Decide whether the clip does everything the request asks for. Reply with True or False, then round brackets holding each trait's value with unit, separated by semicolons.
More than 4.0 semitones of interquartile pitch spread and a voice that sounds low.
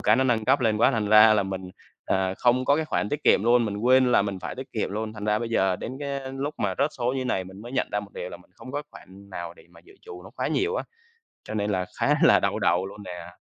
True (4.9 semitones; 110 Hz)